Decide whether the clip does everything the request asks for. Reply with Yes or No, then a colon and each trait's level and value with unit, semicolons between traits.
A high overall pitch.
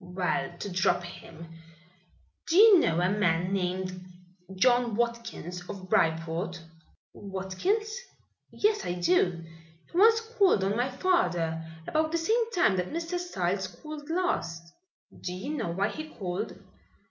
Yes: high, 195 Hz